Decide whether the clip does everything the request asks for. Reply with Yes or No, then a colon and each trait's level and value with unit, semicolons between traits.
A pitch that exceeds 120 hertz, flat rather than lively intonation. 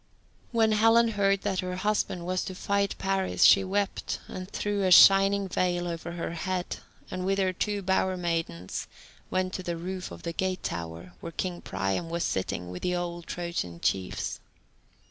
Yes: medium, 185 Hz; narrow, 2.3 semitones